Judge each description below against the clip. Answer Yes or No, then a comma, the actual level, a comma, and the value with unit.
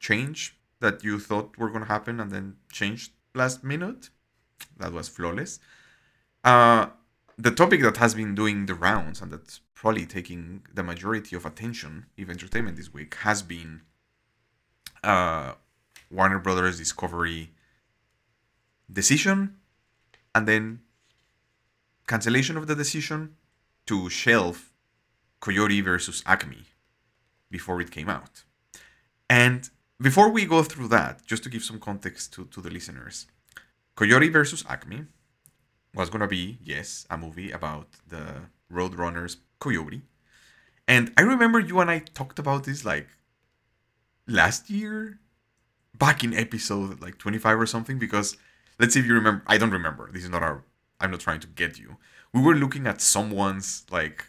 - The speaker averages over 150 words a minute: No, average, 145 wpm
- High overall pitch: No, low, 110 Hz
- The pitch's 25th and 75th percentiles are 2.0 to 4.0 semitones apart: No, average, 4.9 semitones